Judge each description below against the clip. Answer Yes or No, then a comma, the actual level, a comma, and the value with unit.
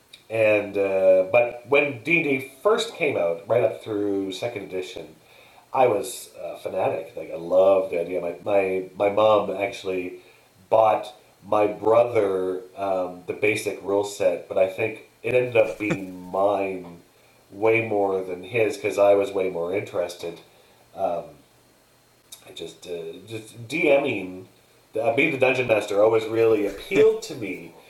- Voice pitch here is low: Yes, low, 100 Hz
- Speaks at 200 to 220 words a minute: No, average, 155 wpm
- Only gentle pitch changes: No, average, 4.0 semitones